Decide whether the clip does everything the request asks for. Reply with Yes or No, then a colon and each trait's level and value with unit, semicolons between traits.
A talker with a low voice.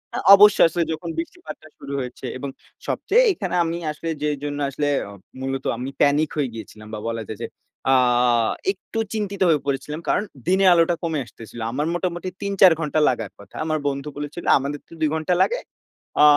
No: medium, 150 Hz